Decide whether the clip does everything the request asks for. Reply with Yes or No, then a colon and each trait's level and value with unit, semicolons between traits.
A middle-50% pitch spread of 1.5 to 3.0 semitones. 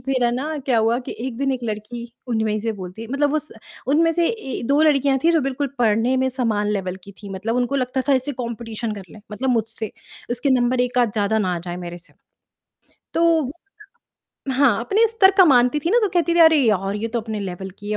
No: average, 4.6 semitones